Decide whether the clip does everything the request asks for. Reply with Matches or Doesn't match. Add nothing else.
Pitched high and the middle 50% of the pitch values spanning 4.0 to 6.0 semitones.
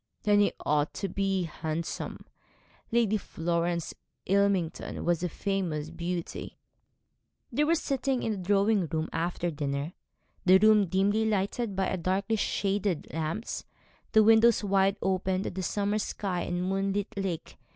Doesn't match